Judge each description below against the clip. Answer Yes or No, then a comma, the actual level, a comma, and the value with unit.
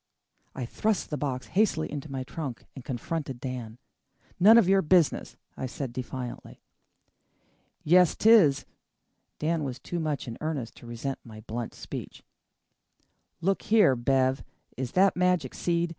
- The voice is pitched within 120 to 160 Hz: Yes, medium, 140 Hz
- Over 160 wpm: No, average, 145 wpm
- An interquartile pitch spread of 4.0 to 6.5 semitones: Yes, wide, 5.5 semitones